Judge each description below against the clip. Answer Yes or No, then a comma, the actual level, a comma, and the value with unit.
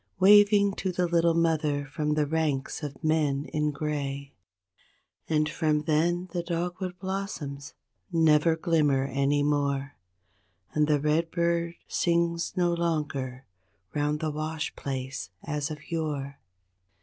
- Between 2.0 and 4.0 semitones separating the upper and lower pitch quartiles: Yes, average, 2.8 semitones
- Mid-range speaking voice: Yes, medium, 155 Hz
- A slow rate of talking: Yes, slow, 125 wpm